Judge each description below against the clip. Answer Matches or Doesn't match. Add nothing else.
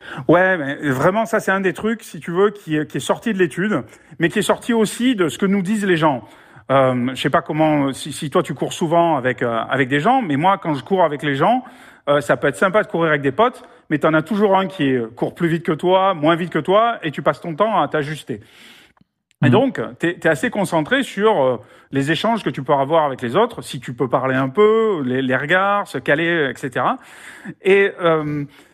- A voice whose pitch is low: Doesn't match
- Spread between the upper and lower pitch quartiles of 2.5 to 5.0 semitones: Doesn't match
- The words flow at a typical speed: Doesn't match